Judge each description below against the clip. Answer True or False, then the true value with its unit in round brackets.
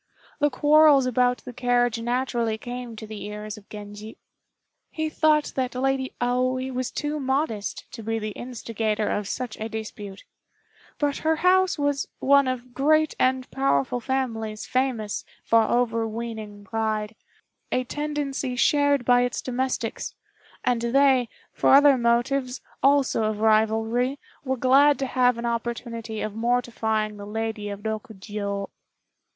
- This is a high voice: True (245 Hz)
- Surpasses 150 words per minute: False (140 wpm)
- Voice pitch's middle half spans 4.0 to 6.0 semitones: False (3.4 semitones)